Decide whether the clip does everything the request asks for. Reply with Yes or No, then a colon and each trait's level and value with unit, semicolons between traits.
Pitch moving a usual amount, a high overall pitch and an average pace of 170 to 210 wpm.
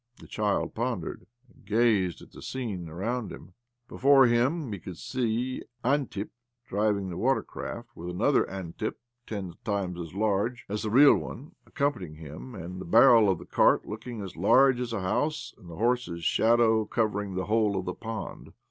No: average, 4.4 semitones; low, 110 Hz; average, 175 wpm